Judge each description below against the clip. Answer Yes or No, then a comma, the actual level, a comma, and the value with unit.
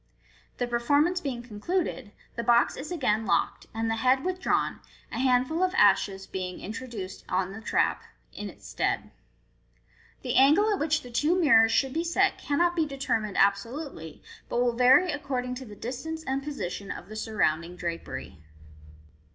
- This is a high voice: Yes, very high, 250 Hz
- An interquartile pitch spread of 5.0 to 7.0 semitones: Yes, wide, 5.6 semitones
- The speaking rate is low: No, average, 165 wpm